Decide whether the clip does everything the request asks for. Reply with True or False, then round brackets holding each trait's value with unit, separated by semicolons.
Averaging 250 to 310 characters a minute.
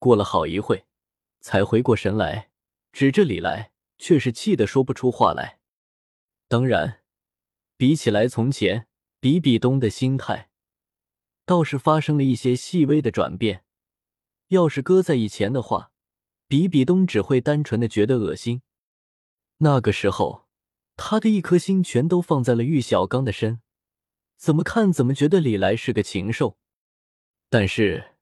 False (215 characters per minute)